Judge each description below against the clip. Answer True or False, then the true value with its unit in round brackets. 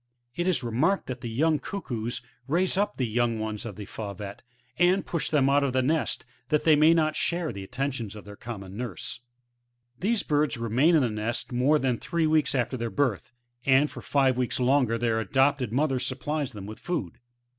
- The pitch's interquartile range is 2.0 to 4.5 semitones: False (4.9 semitones)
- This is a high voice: False (130 Hz)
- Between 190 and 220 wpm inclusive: True (200 wpm)